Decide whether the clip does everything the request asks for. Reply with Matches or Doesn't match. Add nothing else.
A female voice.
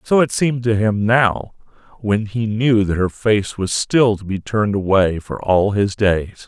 Doesn't match